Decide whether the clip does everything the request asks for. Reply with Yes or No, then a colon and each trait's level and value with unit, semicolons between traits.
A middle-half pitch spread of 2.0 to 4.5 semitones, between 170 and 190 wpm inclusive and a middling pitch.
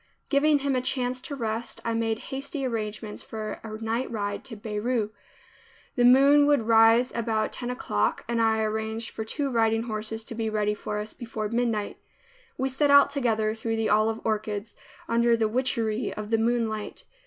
No: narrow, 2.4 semitones; average, 175 wpm; high, 225 Hz